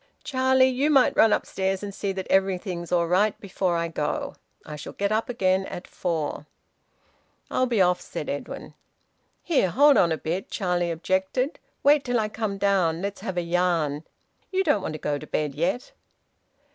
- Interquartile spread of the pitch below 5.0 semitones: Yes, average, 4.6 semitones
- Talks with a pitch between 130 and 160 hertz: No, high, 190 Hz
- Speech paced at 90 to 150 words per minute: No, average, 180 wpm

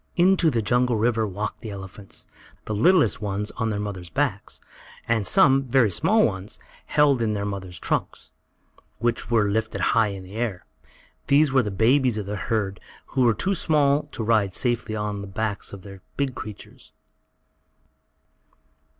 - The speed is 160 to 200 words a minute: Yes, average, 165 wpm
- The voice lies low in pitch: Yes, low, 110 Hz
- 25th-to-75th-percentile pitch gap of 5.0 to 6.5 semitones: No, average, 4.0 semitones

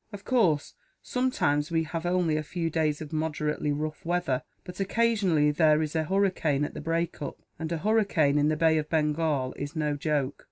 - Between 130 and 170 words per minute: No, average, 195 wpm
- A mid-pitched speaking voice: Yes, medium, 155 Hz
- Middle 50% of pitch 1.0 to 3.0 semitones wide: Yes, average, 2.7 semitones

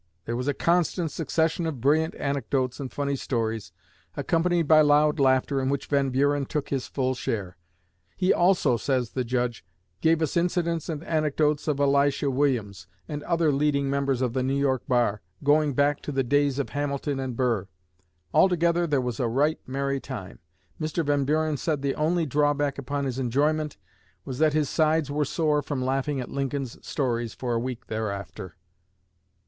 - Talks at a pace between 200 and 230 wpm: No, average, 175 wpm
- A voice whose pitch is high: No, medium, 140 Hz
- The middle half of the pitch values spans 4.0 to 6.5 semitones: No, average, 2.8 semitones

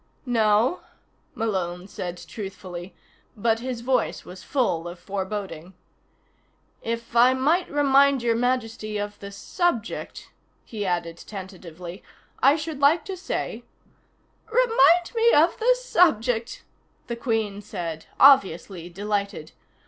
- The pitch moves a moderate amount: No, wide, 6.3 semitones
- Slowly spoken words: Yes, slow, 120 wpm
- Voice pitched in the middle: No, high, 225 Hz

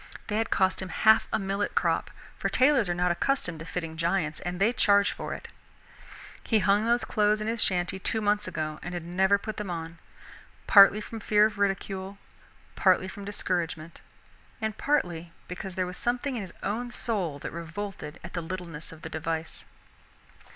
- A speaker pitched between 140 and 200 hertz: Yes, high, 190 Hz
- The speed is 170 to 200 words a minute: Yes, average, 185 wpm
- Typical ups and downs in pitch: Yes, average, 3.6 semitones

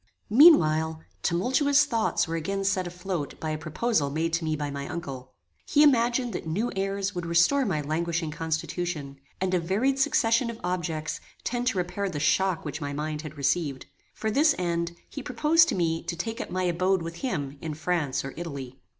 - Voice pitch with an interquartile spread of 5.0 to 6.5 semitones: Yes, wide, 5.6 semitones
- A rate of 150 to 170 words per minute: No, average, 190 wpm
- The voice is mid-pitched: Yes, medium, 175 Hz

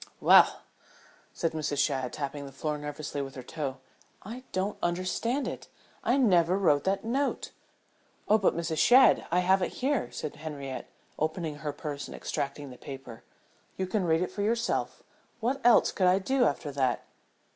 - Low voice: No, medium, 165 Hz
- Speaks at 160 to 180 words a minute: Yes, average, 170 wpm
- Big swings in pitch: Yes, wide, 6.0 semitones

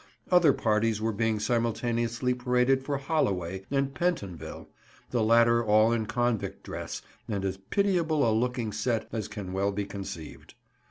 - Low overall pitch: Yes, low, 115 Hz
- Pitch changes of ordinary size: Yes, average, 3.2 semitones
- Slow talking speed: No, average, 150 wpm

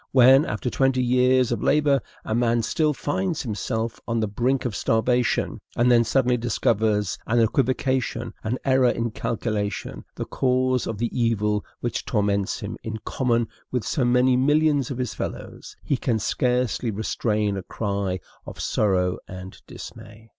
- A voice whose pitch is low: Yes, low, 120 Hz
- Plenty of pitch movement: No, average, 3.0 semitones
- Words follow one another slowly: No, average, 160 wpm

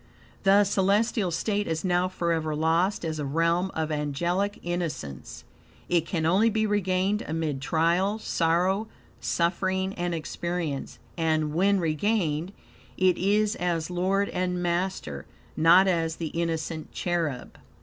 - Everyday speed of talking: No, slow, 130 wpm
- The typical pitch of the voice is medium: Yes, medium, 175 Hz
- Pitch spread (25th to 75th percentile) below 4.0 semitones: Yes, average, 2.9 semitones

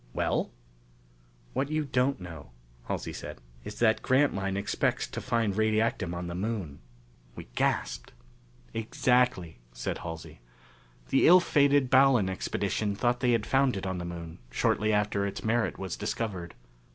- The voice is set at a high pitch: No, low, 110 Hz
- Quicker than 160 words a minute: No, average, 145 wpm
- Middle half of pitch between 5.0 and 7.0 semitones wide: Yes, wide, 5.5 semitones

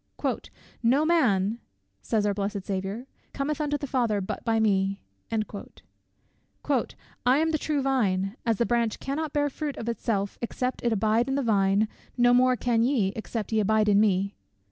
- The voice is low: No, high, 230 Hz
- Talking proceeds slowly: No, average, 165 wpm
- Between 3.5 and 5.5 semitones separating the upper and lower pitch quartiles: Yes, average, 4.4 semitones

